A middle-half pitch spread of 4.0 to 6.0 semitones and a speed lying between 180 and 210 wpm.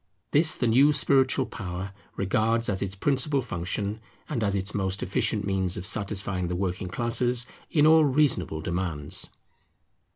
No: wide, 5.5 semitones; average, 150 wpm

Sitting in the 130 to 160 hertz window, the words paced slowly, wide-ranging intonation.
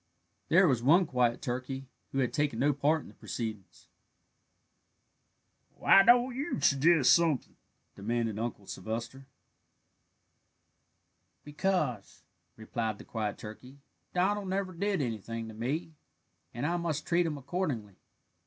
Yes: low, 135 Hz; slow, 125 wpm; wide, 6.6 semitones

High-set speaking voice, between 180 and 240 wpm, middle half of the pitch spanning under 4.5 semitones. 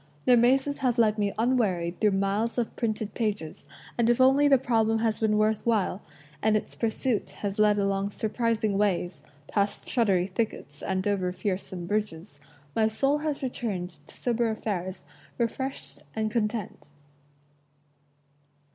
No: high, 215 Hz; average, 145 wpm; average, 3.0 semitones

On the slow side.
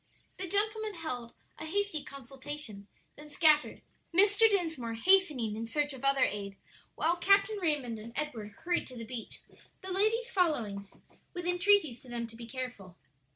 No: average, 155 wpm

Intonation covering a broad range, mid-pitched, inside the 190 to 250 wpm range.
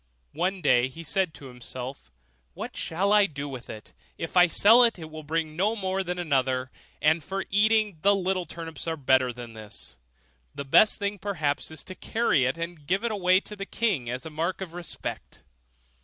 Yes: wide, 5.7 semitones; medium, 165 Hz; average, 195 wpm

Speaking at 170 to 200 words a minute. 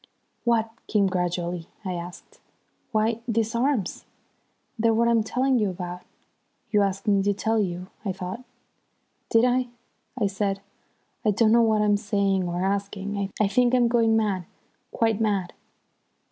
No: average, 150 wpm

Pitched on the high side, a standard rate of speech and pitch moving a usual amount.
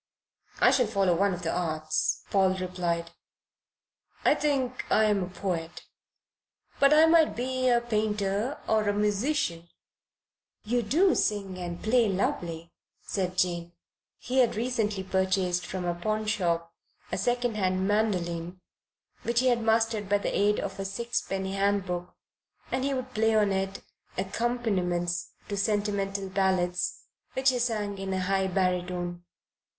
Yes: high, 195 Hz; average, 145 wpm; average, 3.8 semitones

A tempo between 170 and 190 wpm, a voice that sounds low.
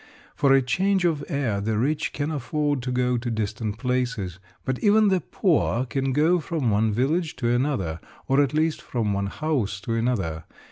Yes: average, 185 wpm; low, 125 Hz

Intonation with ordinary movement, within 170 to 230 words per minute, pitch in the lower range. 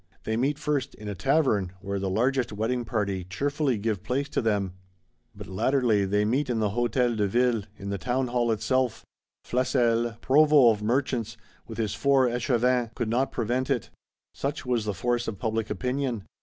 Yes: average, 3.5 semitones; average, 180 wpm; low, 120 Hz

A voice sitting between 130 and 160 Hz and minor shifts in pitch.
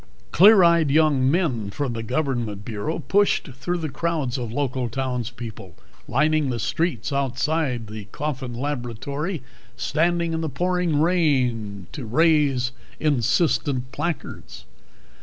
No: medium, 140 Hz; average, 4.8 semitones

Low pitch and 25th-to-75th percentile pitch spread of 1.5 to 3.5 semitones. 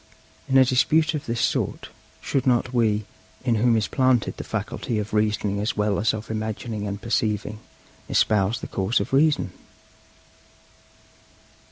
Yes: low, 110 Hz; average, 3.2 semitones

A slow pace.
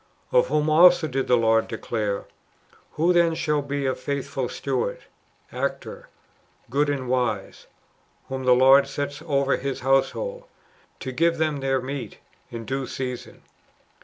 No: average, 150 wpm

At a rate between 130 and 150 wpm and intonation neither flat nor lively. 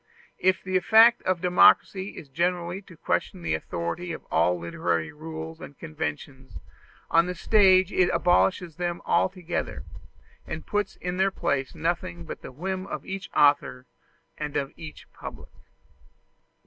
Yes: average, 145 wpm; average, 4.0 semitones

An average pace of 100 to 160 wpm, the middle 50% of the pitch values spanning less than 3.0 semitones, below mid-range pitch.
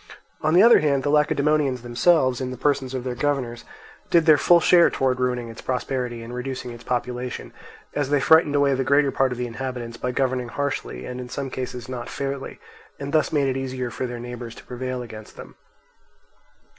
No: average, 200 wpm; narrow, 2.4 semitones; low, 130 Hz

